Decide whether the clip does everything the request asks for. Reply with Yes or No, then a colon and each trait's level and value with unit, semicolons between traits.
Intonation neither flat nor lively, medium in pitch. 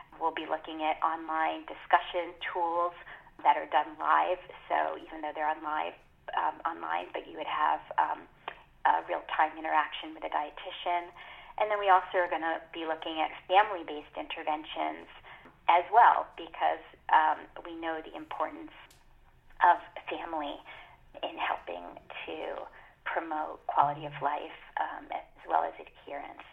No: narrow, 2.3 semitones; medium, 165 Hz